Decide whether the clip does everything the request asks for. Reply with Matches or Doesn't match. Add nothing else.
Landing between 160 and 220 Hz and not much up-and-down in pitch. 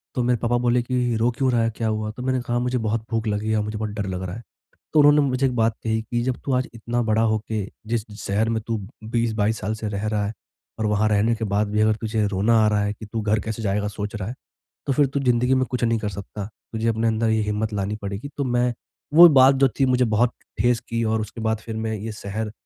Doesn't match